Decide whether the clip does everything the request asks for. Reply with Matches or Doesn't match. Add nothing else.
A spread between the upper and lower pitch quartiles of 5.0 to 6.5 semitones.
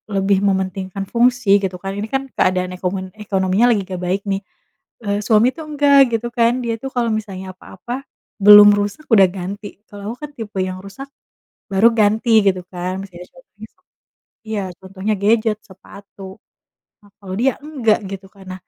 Doesn't match